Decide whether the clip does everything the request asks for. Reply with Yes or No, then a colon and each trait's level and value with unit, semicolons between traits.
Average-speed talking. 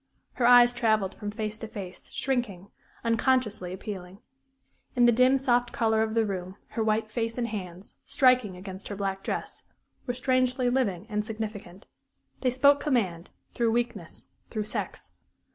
Yes: average, 155 wpm